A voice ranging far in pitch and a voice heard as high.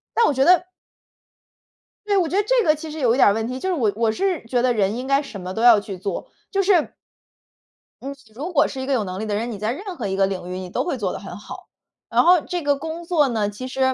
Yes: wide, 7.4 semitones; very high, 255 Hz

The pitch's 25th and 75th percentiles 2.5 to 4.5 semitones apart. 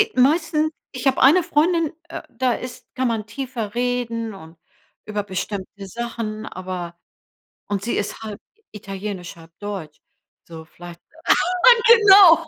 No: average, 5.3 semitones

